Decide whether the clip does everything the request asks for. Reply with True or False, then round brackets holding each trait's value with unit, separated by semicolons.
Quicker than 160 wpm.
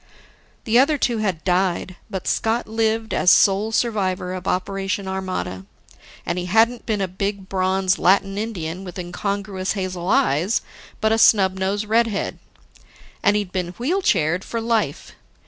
False (150 wpm)